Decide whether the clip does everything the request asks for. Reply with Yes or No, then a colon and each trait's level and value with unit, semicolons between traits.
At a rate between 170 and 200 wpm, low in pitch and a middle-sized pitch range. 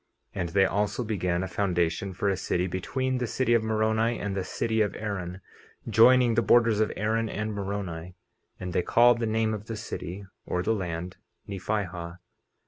Yes: average, 185 wpm; low, 100 Hz; average, 3.5 semitones